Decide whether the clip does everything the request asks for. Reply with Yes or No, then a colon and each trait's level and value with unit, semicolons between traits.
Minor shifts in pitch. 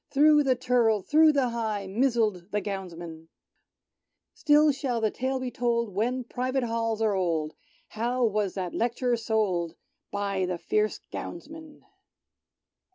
No: average, 4.6 semitones